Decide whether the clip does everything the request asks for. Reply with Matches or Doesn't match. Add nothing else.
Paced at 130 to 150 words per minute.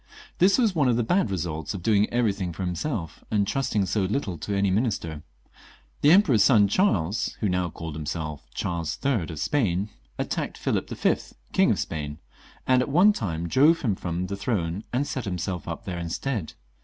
Doesn't match